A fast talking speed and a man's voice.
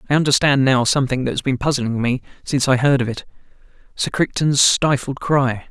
No: average, 180 wpm; male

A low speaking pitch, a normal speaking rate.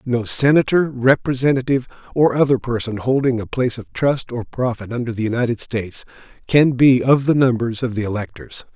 Yes: low, 120 Hz; average, 170 wpm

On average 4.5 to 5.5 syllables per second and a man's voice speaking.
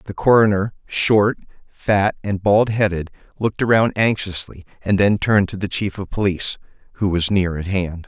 Yes: 5.1 syllables/s; male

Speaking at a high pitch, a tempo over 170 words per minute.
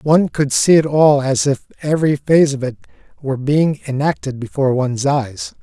No: medium, 140 Hz; average, 180 wpm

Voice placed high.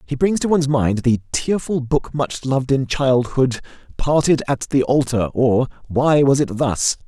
No: low, 135 Hz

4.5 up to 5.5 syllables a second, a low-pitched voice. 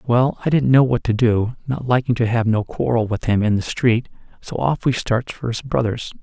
Yes: 5.1 syllables/s; low, 120 Hz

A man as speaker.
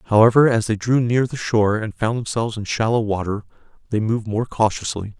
Yes: male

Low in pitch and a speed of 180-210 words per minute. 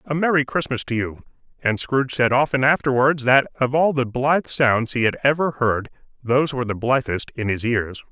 Yes: low, 130 Hz; average, 200 wpm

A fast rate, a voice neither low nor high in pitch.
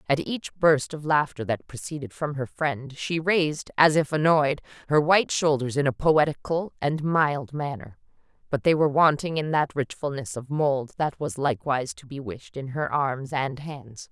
No: average, 185 wpm; medium, 145 Hz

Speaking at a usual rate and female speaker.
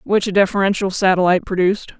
Yes: average, 150 wpm; female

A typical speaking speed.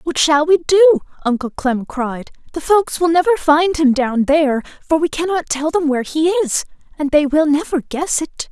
No: fast, 210 wpm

